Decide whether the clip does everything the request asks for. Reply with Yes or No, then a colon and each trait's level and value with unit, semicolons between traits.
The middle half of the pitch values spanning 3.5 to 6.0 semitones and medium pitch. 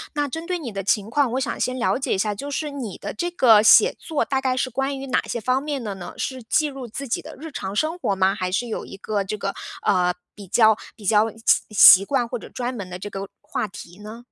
No: average, 5.0 semitones; high, 235 Hz